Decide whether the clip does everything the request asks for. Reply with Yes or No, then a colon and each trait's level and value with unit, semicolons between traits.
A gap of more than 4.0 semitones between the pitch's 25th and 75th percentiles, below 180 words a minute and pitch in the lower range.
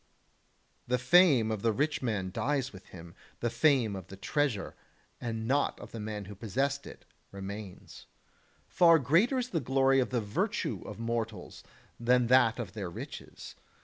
Yes: average, 4.7 semitones; average, 165 wpm; low, 120 Hz